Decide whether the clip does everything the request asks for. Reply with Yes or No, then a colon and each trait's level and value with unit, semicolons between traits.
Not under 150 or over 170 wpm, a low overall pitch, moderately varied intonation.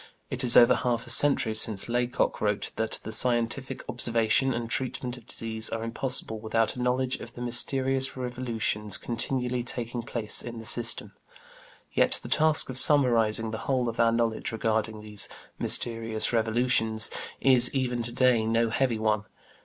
No: average, 160 wpm; low, 120 Hz; narrow, 2.0 semitones